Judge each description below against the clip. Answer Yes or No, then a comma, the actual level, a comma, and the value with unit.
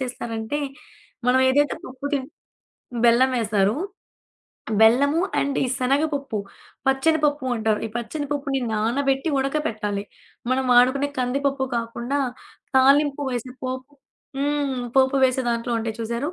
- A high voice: Yes, very high, 260 Hz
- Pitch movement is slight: No, average, 3.2 semitones